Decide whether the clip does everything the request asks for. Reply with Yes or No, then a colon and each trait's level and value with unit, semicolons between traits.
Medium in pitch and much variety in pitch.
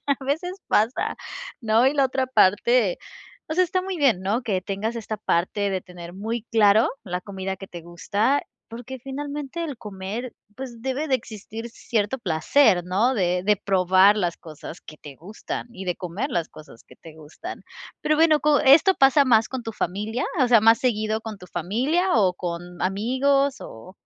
No: high, 220 Hz; wide, 5.9 semitones